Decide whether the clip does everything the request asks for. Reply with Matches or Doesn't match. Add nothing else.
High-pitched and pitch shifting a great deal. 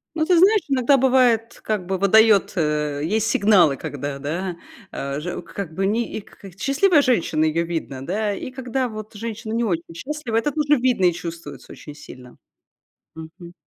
Matches